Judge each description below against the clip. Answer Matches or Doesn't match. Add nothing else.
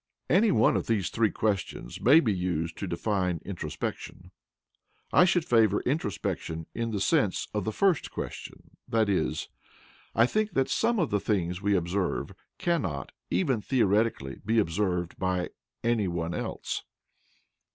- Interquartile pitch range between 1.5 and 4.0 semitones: Doesn't match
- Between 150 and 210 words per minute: Doesn't match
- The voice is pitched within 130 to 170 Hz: Doesn't match